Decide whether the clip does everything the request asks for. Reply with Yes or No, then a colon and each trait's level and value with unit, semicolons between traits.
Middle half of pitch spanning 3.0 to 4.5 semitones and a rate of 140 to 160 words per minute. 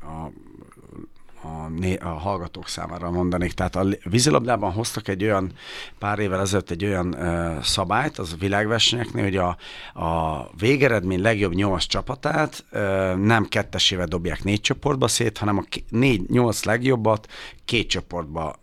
Yes: average, 3.8 semitones; average, 150 wpm